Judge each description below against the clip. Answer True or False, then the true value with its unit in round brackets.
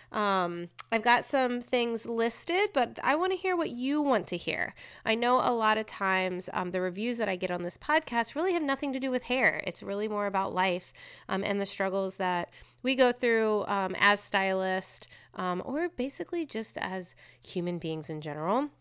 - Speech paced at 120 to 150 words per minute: False (200 wpm)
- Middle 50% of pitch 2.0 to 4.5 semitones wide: False (5.3 semitones)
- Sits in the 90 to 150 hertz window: False (215 Hz)